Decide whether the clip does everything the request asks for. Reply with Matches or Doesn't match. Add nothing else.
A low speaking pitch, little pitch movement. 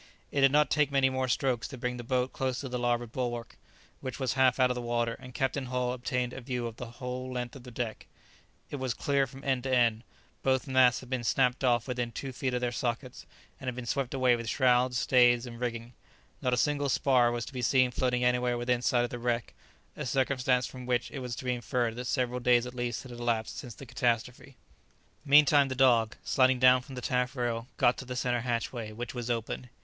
Matches